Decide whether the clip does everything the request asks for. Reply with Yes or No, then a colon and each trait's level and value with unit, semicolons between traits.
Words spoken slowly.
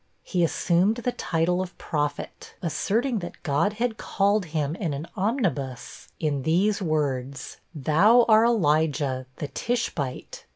Yes: slow, 130 wpm